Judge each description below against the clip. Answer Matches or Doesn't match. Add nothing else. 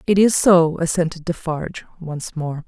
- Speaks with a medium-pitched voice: Matches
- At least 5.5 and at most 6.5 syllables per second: Doesn't match